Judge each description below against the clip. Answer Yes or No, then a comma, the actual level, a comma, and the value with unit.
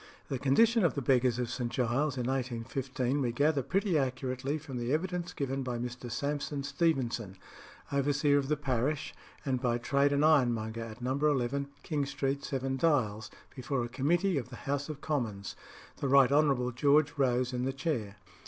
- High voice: No, low, 135 Hz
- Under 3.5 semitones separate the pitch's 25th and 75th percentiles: Yes, average, 2.9 semitones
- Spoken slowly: No, average, 175 wpm